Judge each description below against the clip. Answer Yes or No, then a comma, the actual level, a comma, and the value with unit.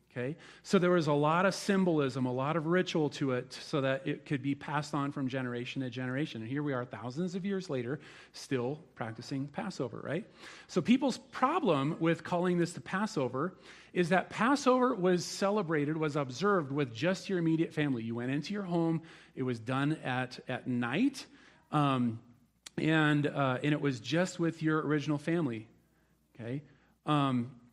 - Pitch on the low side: No, medium, 150 Hz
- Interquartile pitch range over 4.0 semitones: Yes, average, 5.2 semitones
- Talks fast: No, average, 175 wpm